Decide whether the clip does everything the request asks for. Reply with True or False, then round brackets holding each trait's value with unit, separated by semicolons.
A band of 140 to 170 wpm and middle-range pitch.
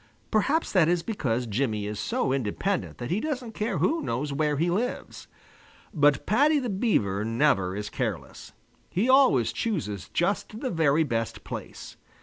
True (155 wpm; 155 Hz)